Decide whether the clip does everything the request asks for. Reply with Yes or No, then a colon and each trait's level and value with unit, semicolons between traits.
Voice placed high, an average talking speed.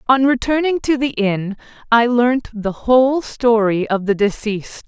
Yes: high, 235 Hz; average, 160 wpm